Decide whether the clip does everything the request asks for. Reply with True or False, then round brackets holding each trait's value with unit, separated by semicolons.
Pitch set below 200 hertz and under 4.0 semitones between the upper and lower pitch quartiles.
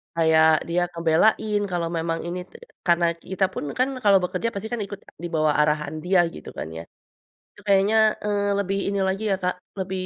True (185 Hz; 3.4 semitones)